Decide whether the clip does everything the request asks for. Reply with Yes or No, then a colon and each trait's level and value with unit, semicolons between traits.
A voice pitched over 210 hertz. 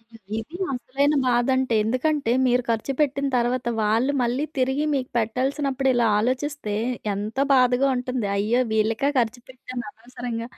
Yes: very high, 250 Hz